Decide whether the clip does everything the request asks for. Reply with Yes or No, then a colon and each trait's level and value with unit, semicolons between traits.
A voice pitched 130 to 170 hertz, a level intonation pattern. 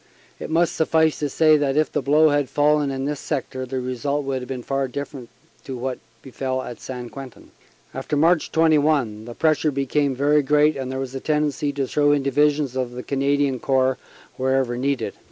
Yes: medium, 140 Hz; narrow, 2.3 semitones